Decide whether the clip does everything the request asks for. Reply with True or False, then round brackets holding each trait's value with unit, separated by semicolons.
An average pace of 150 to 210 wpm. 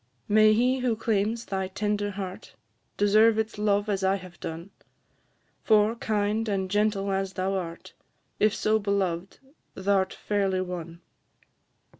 False (140 wpm)